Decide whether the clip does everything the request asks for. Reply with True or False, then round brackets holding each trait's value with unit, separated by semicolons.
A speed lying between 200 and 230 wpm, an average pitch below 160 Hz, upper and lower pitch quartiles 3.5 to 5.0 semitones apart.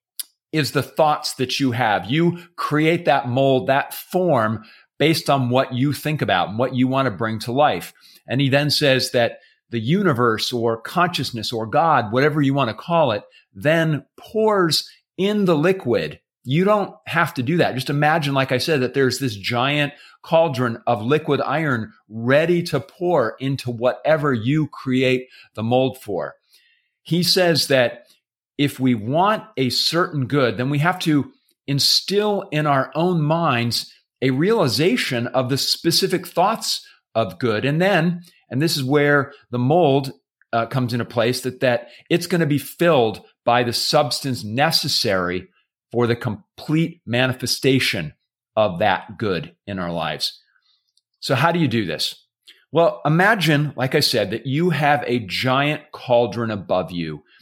False (160 wpm; 135 Hz; 4.4 semitones)